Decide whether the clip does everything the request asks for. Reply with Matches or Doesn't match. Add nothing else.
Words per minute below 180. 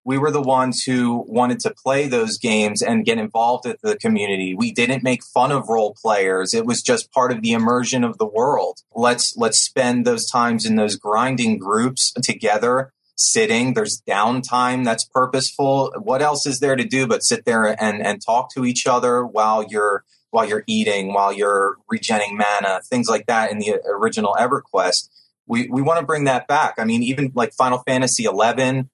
Doesn't match